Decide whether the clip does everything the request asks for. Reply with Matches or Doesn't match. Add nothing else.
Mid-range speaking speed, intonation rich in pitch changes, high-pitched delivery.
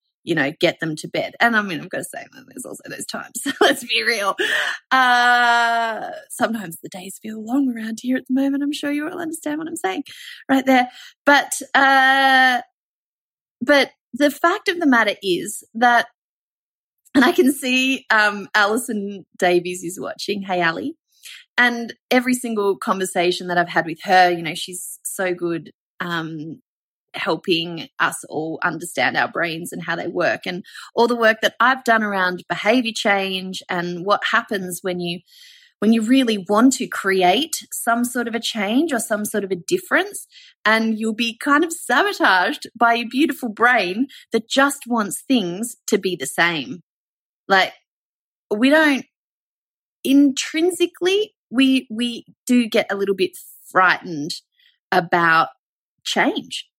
Matches